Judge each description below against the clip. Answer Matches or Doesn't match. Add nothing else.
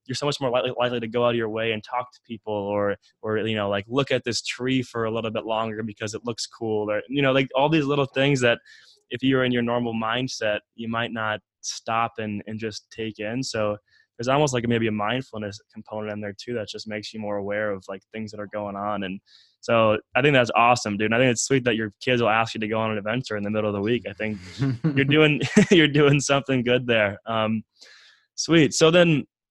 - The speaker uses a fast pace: Matches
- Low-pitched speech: Matches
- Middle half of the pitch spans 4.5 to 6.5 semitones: Doesn't match